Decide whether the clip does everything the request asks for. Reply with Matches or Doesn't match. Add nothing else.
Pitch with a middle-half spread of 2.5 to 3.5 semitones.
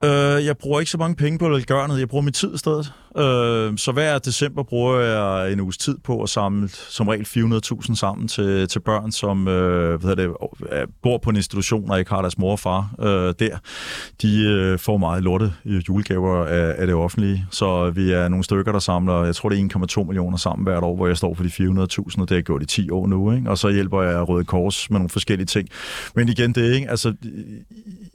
Doesn't match